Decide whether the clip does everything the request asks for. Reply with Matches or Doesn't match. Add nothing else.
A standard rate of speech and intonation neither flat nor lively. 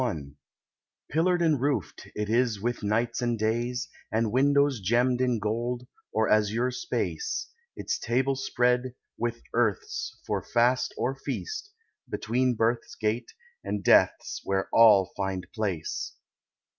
Doesn't match